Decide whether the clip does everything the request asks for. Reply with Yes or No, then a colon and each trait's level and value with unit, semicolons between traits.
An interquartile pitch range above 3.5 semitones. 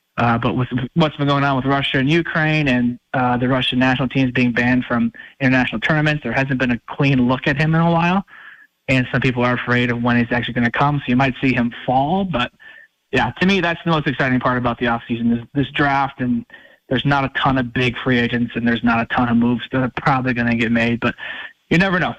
No: average, 2.7 semitones